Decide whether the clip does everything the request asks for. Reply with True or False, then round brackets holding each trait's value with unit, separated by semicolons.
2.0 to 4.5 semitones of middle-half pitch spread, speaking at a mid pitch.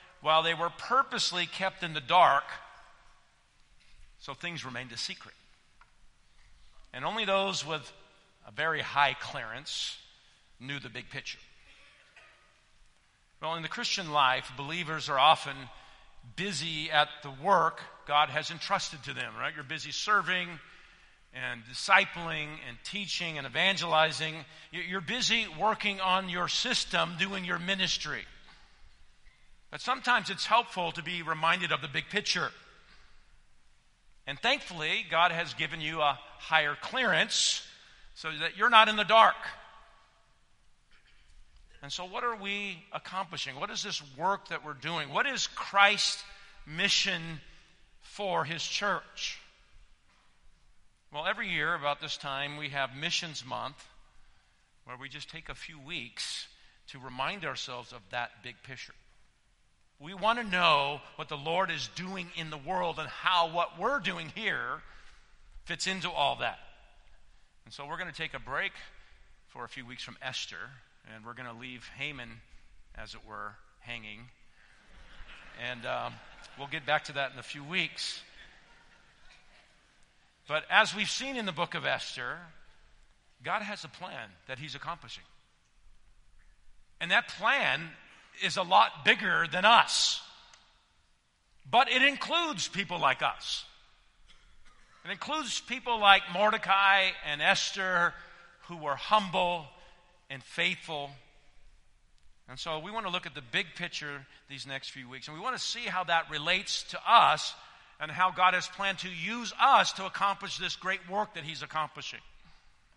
False (5.2 semitones; 165 Hz)